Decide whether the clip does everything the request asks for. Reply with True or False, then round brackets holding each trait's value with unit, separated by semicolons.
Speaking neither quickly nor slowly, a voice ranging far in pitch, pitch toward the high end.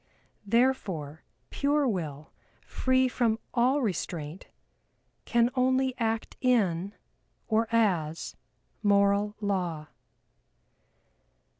False (80 wpm; 6.2 semitones; 215 Hz)